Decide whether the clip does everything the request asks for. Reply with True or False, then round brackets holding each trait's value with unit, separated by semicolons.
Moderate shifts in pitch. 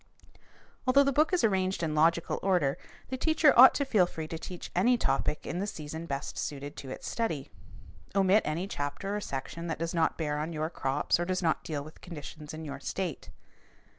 True (4.4 semitones)